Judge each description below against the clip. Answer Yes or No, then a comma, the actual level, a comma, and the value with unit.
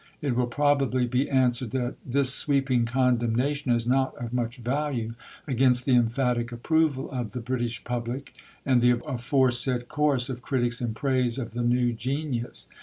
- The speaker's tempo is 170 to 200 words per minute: No, average, 160 wpm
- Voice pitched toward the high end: No, low, 125 Hz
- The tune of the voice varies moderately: No, narrow, 2.0 semitones